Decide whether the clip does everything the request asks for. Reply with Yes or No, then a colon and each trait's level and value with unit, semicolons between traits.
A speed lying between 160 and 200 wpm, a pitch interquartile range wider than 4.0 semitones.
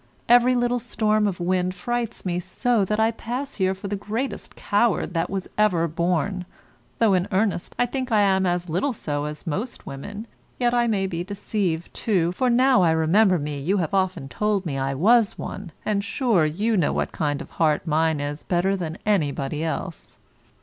Yes: average, 190 wpm; average, 4.9 semitones